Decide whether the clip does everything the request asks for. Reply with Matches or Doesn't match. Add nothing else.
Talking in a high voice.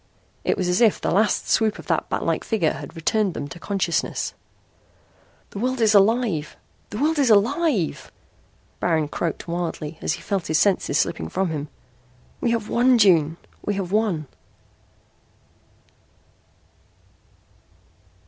Matches